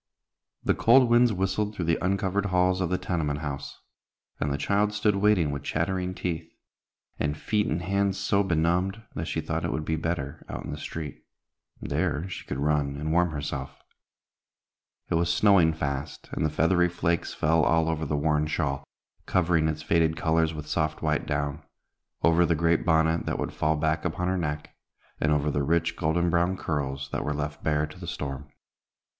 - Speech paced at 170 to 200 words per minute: Yes, average, 185 wpm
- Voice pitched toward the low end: Yes, very low, 80 Hz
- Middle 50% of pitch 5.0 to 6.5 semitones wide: No, average, 3.3 semitones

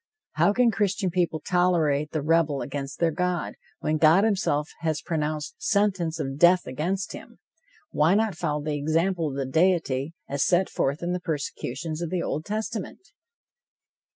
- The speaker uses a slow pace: No, average, 160 wpm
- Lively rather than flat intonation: No, average, 3.6 semitones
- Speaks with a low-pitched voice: No, medium, 165 Hz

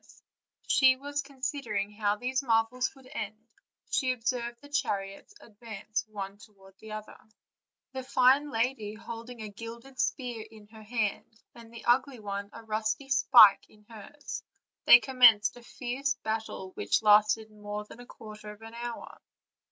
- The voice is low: No, high, 225 Hz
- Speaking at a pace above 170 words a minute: No, average, 160 wpm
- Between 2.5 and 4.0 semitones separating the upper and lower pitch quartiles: Yes, average, 3.0 semitones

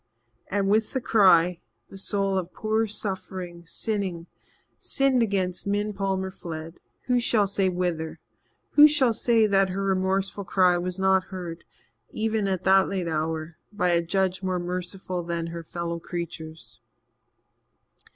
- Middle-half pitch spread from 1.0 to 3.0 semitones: Yes, narrow, 2.6 semitones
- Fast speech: No, average, 140 wpm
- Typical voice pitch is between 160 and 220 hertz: Yes, high, 190 Hz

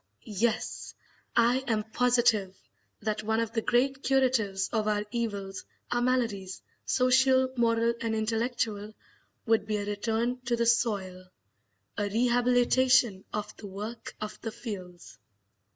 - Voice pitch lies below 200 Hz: No, high, 225 Hz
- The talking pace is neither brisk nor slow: No, slow, 130 wpm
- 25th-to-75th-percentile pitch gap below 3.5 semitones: Yes, average, 2.8 semitones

